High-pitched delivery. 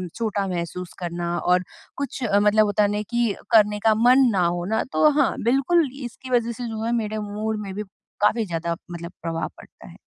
Yes: high, 210 Hz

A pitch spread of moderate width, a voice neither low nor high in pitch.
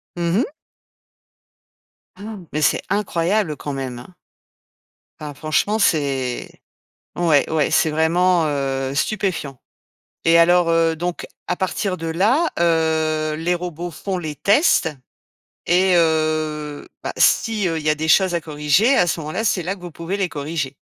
Yes: average, 3.0 semitones; medium, 165 Hz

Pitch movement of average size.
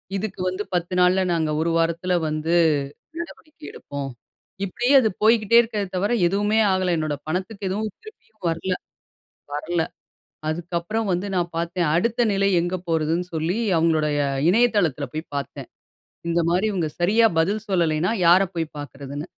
Yes: average, 4.1 semitones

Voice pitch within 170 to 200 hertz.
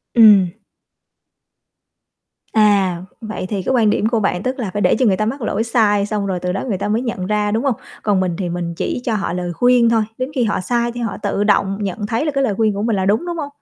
No: high, 210 Hz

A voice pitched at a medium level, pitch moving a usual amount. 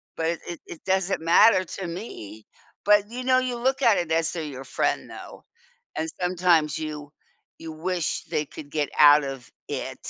Yes: medium, 165 Hz; average, 4.1 semitones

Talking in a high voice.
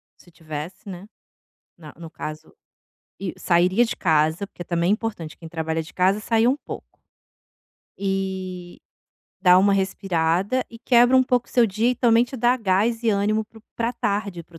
Yes: high, 195 Hz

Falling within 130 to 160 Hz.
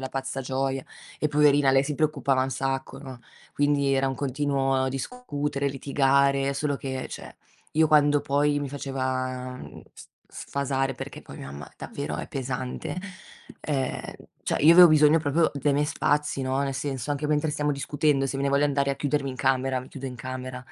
Yes: medium, 140 Hz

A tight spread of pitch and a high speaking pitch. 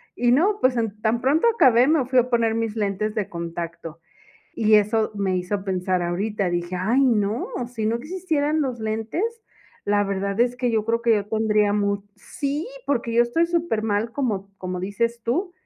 No: average, 3.6 semitones; high, 220 Hz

